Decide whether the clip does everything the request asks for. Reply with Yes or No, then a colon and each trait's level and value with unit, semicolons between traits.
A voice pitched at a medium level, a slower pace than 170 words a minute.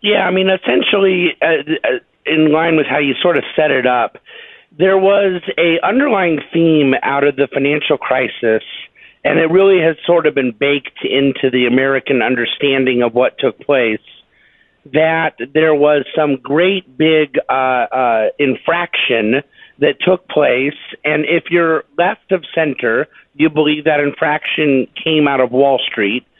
Yes: medium, 155 Hz; average, 155 wpm